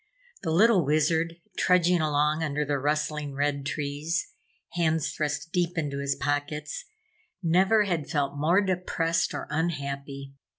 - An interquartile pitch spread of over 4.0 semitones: No, average, 2.8 semitones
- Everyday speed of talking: No, slow, 130 wpm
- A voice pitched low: No, medium, 155 Hz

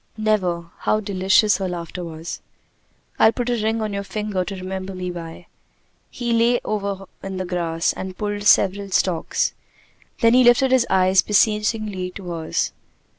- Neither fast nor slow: Yes, average, 160 wpm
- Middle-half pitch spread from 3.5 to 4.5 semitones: No, average, 2.8 semitones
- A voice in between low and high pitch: No, high, 195 Hz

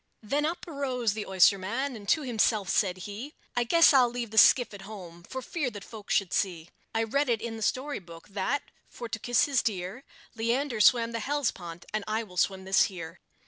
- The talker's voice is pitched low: No, high, 225 Hz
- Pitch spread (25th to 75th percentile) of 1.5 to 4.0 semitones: No, average, 4.8 semitones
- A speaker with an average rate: No, fast, 210 wpm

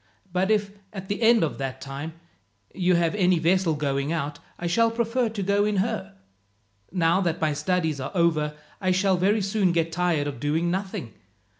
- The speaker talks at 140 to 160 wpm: No, average, 185 wpm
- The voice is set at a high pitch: No, medium, 180 Hz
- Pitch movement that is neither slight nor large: Yes, average, 4.1 semitones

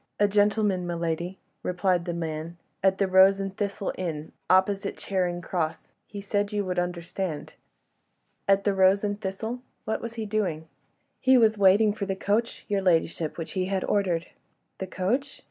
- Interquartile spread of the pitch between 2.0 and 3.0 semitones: Yes, narrow, 2.5 semitones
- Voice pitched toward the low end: No, high, 190 Hz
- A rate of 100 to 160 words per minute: No, average, 170 wpm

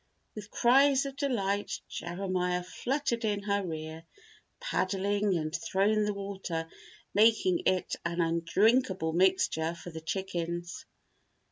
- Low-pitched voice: No, high, 190 Hz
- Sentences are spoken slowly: Yes, slow, 115 wpm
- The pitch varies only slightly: No, average, 3.5 semitones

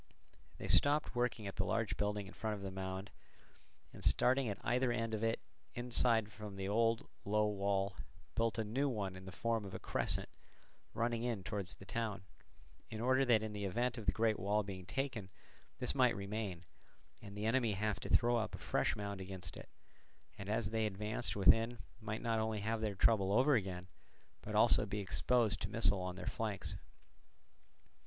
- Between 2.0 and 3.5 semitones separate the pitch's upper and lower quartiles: Yes, average, 2.7 semitones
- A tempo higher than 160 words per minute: Yes, average, 190 wpm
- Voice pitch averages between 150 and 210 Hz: No, low, 105 Hz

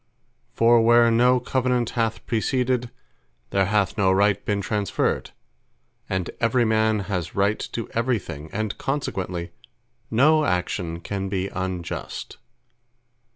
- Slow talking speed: Yes, slow, 120 wpm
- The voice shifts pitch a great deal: No, average, 3.8 semitones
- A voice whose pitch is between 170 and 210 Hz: No, low, 105 Hz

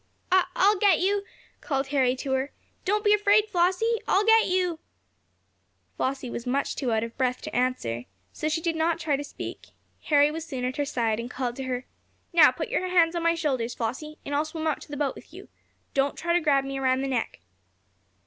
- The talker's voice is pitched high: Yes, very high, 290 Hz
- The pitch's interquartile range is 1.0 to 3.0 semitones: No, average, 5.2 semitones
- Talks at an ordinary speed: No, fast, 215 wpm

